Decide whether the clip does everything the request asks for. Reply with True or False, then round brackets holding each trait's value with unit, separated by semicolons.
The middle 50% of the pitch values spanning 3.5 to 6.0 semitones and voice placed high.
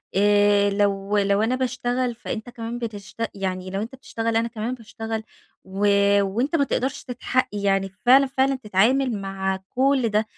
True (3.8 semitones; 225 Hz)